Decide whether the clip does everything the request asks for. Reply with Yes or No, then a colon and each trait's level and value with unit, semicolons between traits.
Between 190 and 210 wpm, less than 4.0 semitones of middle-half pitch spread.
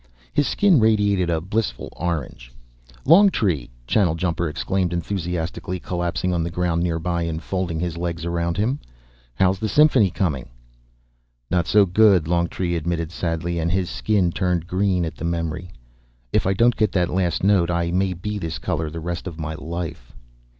No: average, 165 wpm; narrow, 2.4 semitones